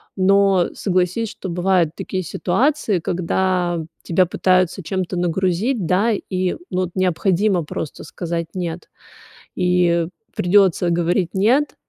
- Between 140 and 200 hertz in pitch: Yes, medium, 185 Hz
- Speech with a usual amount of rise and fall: No, narrow, 1.8 semitones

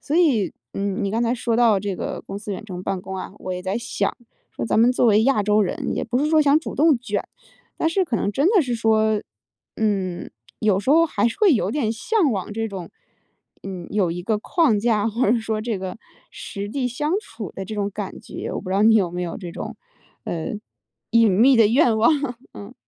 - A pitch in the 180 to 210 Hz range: No, high, 220 Hz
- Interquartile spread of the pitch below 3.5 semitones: No, average, 3.8 semitones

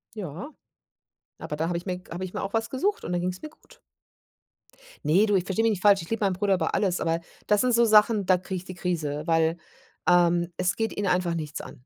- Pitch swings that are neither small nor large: Yes, average, 3.4 semitones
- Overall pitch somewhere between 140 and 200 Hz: Yes, medium, 185 Hz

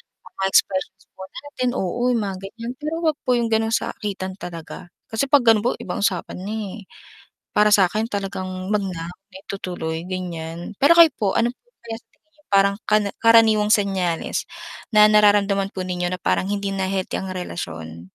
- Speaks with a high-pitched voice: Yes, high, 200 Hz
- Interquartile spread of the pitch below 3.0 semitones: No, average, 3.4 semitones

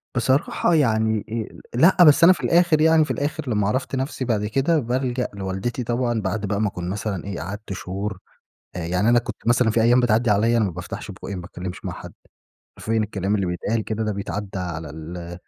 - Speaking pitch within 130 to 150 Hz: No, low, 110 Hz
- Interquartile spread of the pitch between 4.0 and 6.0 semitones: Yes, average, 4.5 semitones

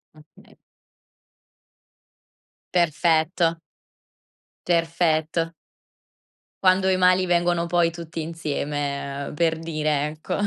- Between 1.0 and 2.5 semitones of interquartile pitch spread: Yes, narrow, 2.0 semitones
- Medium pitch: Yes, medium, 165 Hz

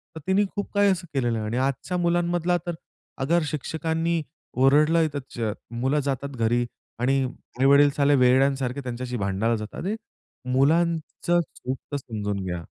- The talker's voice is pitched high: No, medium, 140 Hz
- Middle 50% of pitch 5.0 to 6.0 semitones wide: Yes, wide, 5.4 semitones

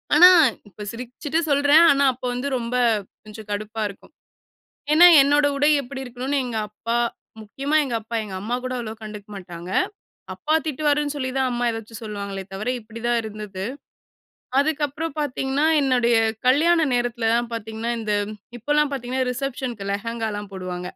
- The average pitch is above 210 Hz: Yes, high, 240 Hz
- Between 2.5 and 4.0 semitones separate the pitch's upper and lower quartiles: No, average, 4.6 semitones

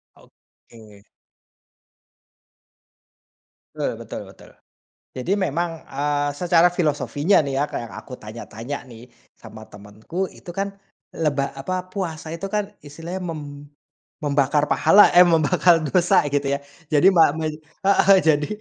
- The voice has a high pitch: No, medium, 155 Hz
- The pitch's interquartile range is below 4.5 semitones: Yes, average, 4.1 semitones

